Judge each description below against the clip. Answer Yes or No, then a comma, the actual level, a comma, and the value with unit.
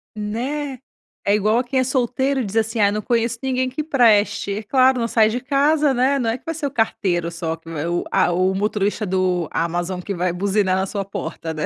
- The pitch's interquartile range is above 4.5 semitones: Yes, wide, 5.5 semitones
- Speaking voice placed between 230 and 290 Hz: No, high, 215 Hz